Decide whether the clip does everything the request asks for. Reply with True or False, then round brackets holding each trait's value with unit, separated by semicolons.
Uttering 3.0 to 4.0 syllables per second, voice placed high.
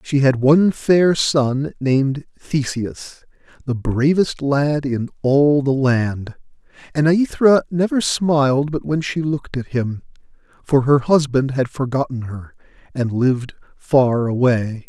False (3.9 syllables/s; 140 Hz)